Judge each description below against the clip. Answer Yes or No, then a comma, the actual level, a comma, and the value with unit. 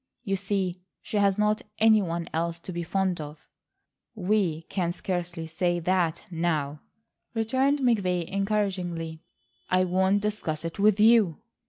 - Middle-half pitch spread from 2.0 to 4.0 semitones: Yes, average, 3.5 semitones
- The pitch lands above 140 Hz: Yes, medium, 185 Hz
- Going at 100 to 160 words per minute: Yes, average, 140 wpm